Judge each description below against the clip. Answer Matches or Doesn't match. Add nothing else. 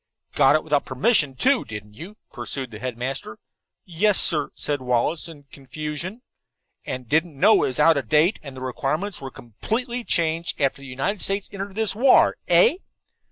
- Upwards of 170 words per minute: Matches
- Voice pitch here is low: Doesn't match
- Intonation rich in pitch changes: Matches